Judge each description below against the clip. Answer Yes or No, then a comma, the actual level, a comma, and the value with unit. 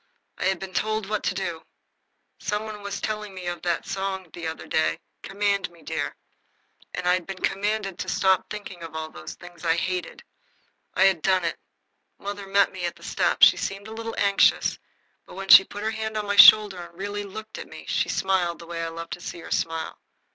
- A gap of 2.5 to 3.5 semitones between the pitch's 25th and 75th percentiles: Yes, average, 2.9 semitones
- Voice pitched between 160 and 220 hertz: Yes, high, 190 Hz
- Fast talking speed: Yes, fast, 220 wpm